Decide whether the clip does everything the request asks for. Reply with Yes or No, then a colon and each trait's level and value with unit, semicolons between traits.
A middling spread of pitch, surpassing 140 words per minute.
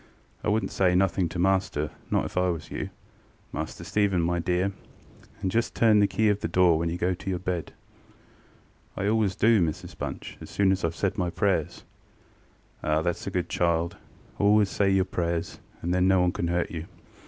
No: narrow, 2.3 semitones; average, 200 wpm